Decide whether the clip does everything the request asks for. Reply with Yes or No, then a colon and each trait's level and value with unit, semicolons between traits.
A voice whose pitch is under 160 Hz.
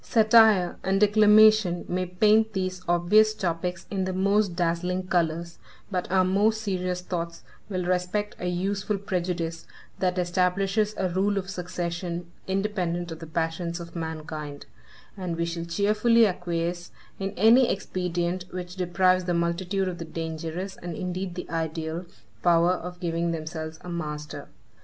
No: medium, 180 Hz